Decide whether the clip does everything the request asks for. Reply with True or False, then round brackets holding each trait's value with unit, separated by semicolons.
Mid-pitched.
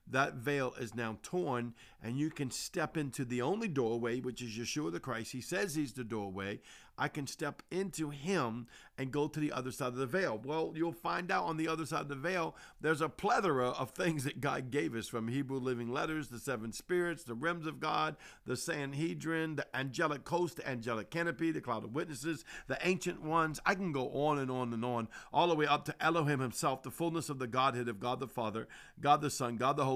True (145 Hz)